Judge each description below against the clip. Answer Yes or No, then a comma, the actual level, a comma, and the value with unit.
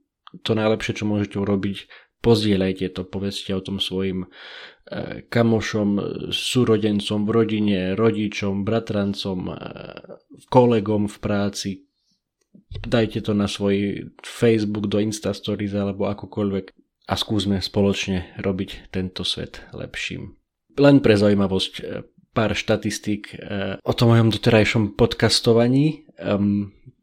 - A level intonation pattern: Yes, narrow, 2.1 semitones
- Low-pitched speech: Yes, low, 105 Hz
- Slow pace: Yes, slow, 100 wpm